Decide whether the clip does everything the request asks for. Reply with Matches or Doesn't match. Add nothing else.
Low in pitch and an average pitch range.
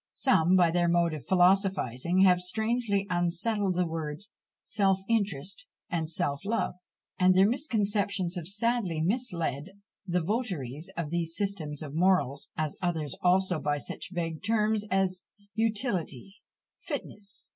Doesn't match